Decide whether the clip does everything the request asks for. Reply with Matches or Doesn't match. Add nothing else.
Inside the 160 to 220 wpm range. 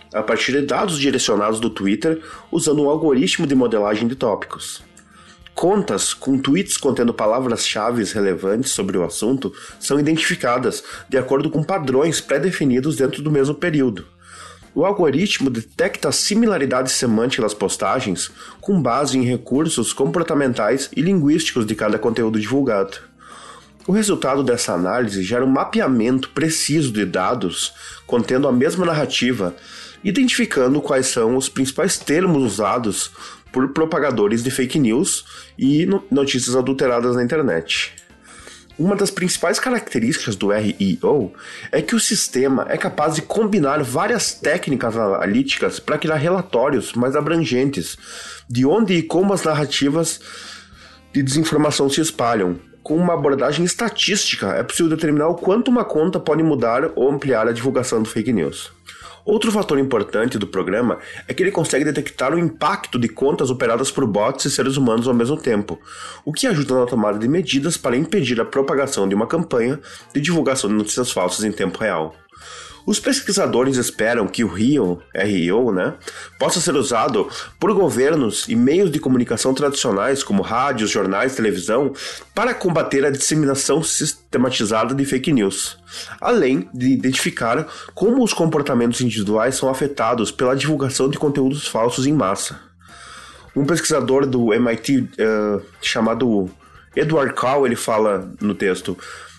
Doesn't match